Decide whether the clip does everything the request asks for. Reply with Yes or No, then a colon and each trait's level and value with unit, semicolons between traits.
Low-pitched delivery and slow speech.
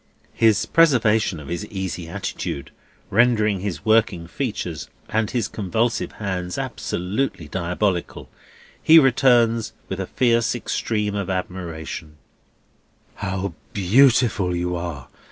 Yes: low, 100 Hz; slow, 110 wpm